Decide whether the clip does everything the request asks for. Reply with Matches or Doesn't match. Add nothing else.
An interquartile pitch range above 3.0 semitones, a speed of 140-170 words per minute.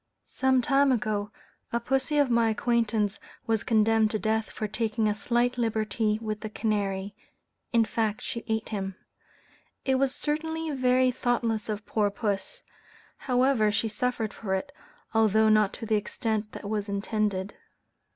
Doesn't match